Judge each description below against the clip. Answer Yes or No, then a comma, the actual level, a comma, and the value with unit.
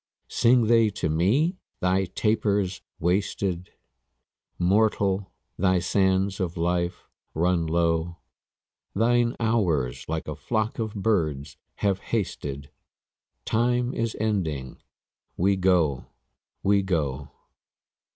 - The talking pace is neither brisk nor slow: No, slow, 100 wpm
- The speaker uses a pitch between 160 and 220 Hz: No, very low, 95 Hz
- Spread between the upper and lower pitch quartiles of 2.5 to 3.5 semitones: No, average, 4.5 semitones